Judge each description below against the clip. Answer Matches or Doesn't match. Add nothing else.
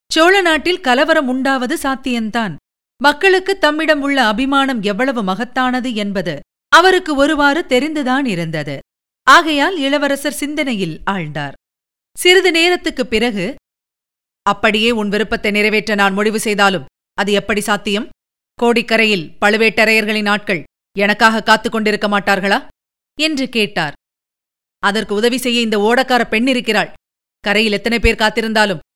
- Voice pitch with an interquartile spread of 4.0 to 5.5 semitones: Matches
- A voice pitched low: Doesn't match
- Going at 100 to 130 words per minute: Matches